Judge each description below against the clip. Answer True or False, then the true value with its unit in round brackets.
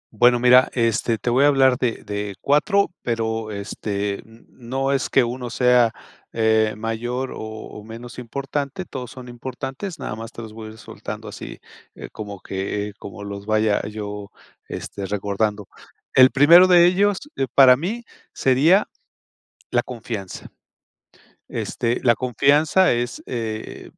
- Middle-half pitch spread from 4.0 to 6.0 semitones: False (3.6 semitones)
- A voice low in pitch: True (120 Hz)